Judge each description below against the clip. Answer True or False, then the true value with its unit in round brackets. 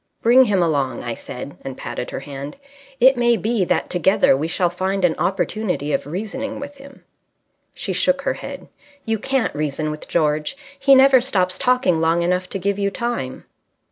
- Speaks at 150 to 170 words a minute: False (180 wpm)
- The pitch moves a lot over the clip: True (7.8 semitones)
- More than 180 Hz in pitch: True (190 Hz)